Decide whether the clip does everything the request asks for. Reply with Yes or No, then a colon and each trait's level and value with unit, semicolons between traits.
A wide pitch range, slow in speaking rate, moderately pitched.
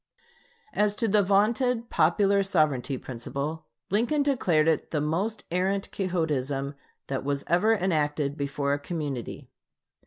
Yes: wide, 6.1 semitones; slow, 125 wpm; medium, 165 Hz